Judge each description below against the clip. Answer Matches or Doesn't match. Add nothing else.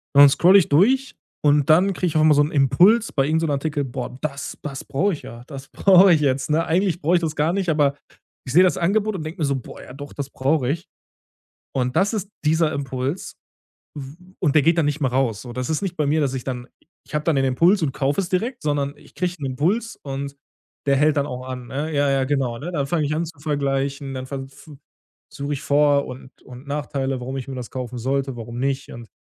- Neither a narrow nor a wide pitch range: Matches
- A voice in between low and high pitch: Matches